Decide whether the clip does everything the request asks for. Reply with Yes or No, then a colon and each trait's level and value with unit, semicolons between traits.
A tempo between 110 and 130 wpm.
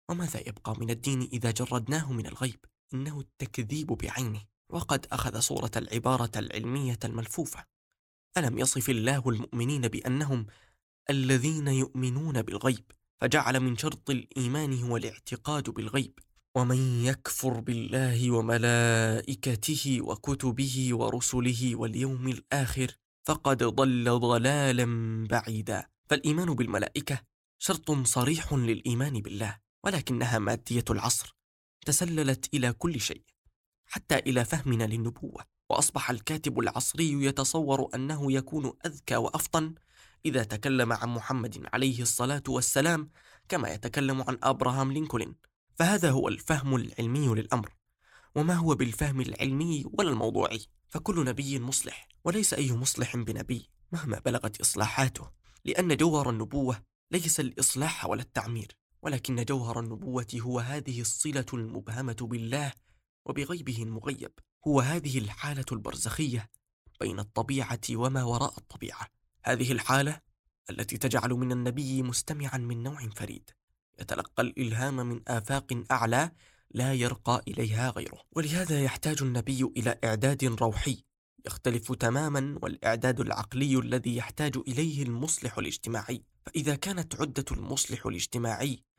Yes: average, 115 wpm